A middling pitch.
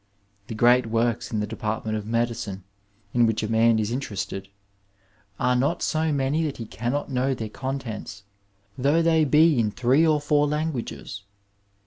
No: low, 120 Hz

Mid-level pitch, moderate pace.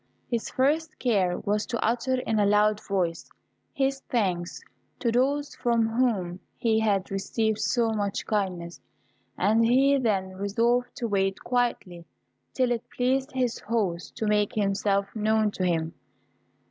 No: high, 220 Hz; average, 145 wpm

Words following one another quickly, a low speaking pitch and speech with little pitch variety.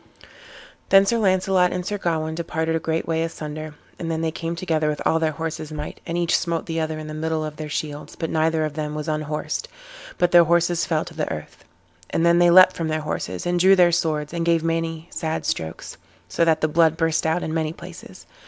No: fast, 225 wpm; medium, 160 Hz; narrow, 1.6 semitones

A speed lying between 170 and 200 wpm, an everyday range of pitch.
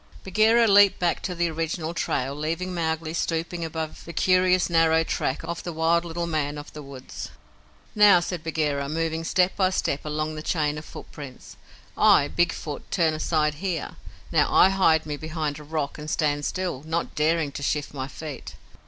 No: average, 180 wpm; narrow, 2.3 semitones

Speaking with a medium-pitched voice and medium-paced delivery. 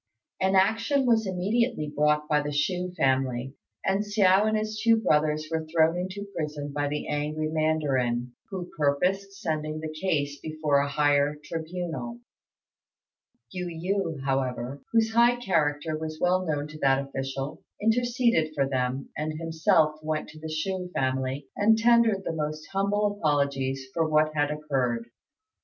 Yes: medium, 155 Hz; average, 150 wpm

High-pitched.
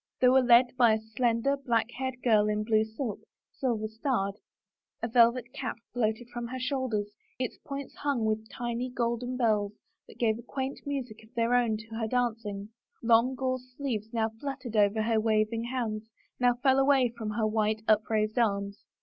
Yes: high, 230 Hz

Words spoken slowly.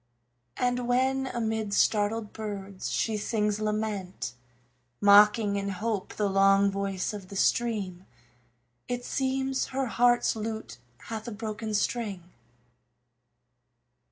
Yes: slow, 110 wpm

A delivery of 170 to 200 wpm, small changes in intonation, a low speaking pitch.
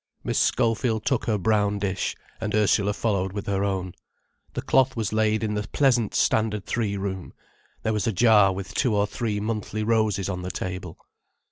Yes: average, 180 wpm; narrow, 2.2 semitones; low, 105 Hz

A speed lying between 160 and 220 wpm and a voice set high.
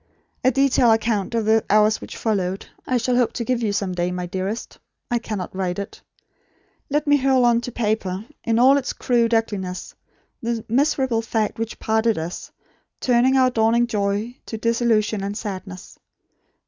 Yes: average, 170 wpm; high, 225 Hz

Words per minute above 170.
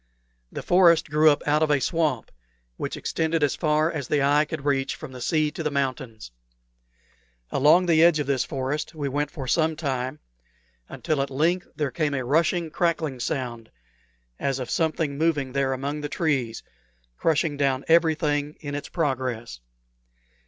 No: average, 165 wpm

